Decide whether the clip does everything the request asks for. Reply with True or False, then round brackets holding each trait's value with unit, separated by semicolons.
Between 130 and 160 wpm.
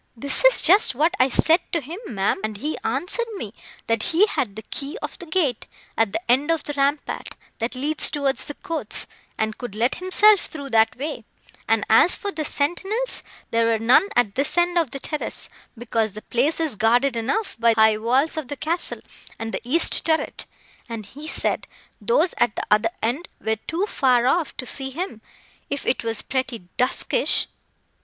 False (195 wpm)